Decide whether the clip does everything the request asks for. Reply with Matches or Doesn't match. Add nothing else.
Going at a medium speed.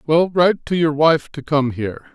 Doesn't match